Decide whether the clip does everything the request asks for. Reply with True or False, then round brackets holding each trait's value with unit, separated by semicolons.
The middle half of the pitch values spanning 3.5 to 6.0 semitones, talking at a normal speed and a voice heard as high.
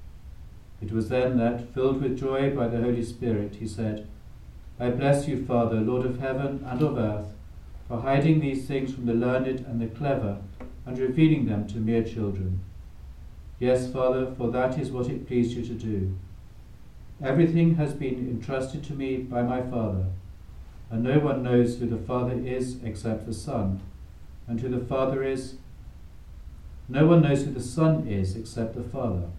False (4.1 semitones; 175 wpm; 120 Hz)